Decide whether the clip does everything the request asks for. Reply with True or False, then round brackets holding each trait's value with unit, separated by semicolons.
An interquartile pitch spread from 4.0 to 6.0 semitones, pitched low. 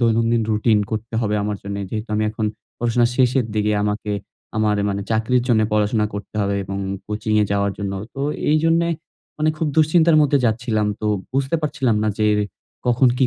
False (3.4 semitones; 110 Hz)